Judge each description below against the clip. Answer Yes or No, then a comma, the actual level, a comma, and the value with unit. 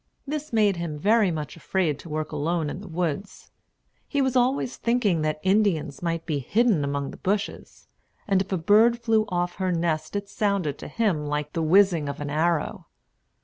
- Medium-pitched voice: Yes, medium, 175 Hz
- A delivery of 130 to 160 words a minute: No, average, 190 wpm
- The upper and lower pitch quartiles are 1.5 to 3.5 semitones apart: No, average, 5.1 semitones